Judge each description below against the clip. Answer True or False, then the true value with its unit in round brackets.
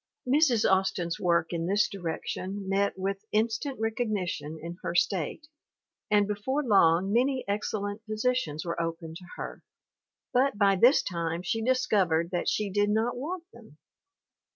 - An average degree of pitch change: True (4.6 semitones)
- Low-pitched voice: False (200 Hz)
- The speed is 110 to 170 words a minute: True (150 wpm)